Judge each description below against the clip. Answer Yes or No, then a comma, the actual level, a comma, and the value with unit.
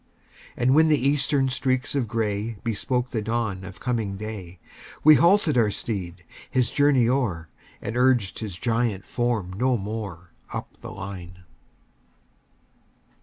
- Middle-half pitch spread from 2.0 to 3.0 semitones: No, average, 4.6 semitones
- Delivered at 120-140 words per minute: Yes, slow, 135 wpm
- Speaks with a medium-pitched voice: No, low, 115 Hz